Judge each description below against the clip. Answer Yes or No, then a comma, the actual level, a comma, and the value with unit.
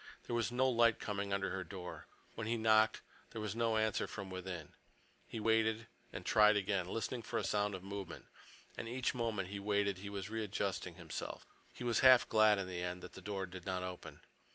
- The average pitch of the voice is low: Yes, low, 105 Hz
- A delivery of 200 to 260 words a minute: Yes, fast, 205 wpm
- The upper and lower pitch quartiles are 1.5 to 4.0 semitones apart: Yes, average, 2.9 semitones